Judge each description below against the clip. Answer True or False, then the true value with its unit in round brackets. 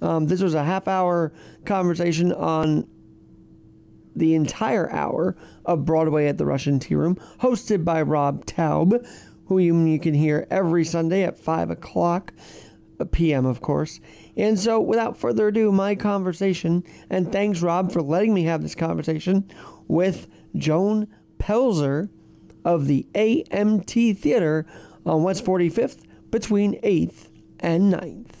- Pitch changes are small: False (3.6 semitones)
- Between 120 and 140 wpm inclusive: True (135 wpm)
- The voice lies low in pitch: False (175 Hz)